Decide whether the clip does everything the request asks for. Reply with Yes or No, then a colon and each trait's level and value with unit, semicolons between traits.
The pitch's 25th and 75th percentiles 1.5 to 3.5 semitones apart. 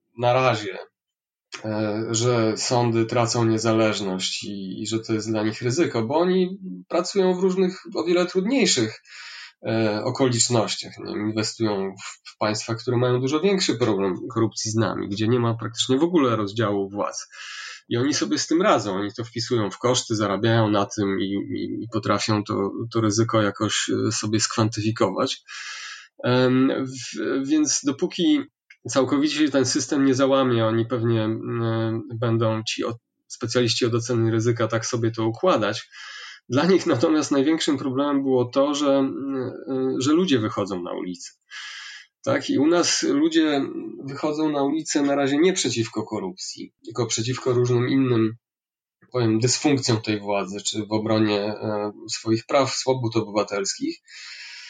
No: average, 4.1 semitones